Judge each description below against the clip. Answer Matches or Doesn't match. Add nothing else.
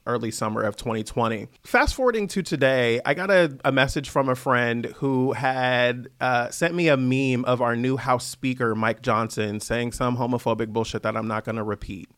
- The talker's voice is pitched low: Matches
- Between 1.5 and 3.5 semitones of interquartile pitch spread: Matches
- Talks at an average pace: Matches